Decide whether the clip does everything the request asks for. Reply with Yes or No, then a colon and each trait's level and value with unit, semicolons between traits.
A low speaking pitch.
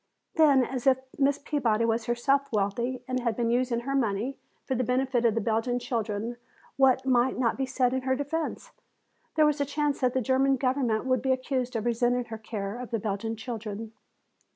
No: very high, 250 Hz